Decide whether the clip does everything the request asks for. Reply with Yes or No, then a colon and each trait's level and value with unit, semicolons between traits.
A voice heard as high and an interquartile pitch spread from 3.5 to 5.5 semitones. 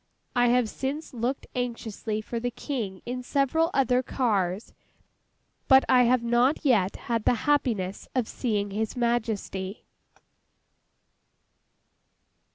No: high, 240 Hz; average, 2.9 semitones